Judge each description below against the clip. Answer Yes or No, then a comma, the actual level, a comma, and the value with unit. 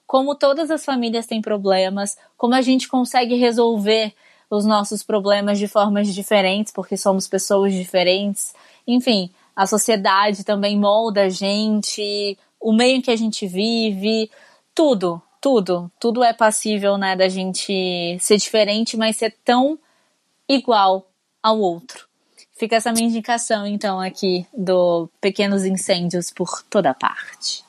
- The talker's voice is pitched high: Yes, high, 210 Hz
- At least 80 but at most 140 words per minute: Yes, average, 135 wpm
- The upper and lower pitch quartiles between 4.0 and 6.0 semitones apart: No, average, 3.1 semitones